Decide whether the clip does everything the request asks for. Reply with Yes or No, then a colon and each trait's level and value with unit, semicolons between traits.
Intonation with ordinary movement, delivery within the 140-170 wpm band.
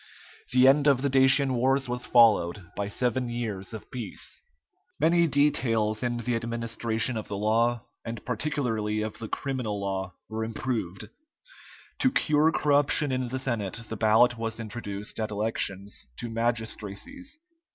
Yes: average, 3.5 semitones; average, 145 wpm